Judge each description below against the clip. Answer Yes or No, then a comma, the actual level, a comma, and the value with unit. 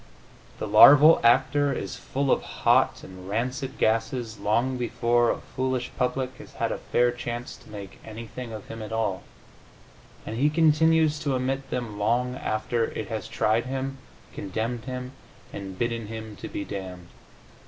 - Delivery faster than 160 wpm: No, average, 155 wpm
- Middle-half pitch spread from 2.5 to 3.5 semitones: Yes, average, 3.1 semitones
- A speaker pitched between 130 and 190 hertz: No, low, 120 Hz